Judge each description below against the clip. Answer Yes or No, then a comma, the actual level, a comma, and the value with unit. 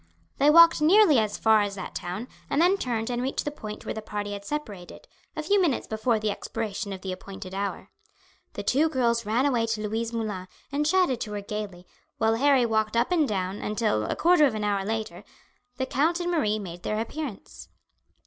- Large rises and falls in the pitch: Yes, wide, 5.7 semitones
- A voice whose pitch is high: Yes, high, 225 Hz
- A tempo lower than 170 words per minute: No, fast, 205 wpm